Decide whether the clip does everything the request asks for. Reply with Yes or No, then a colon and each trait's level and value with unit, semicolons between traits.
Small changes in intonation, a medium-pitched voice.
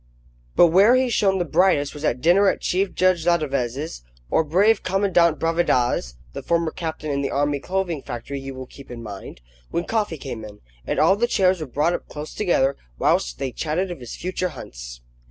No: wide, 5.4 semitones; medium, 160 Hz